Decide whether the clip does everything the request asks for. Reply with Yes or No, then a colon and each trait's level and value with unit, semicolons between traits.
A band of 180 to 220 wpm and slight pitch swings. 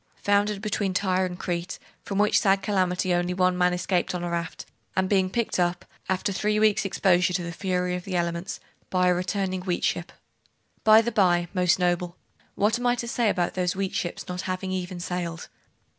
Yes: average, 200 wpm; narrow, 1.9 semitones